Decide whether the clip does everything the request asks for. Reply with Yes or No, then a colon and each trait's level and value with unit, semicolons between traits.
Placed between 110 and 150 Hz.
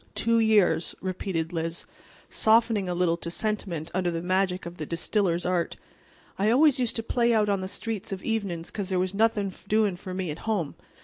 No: high, 190 Hz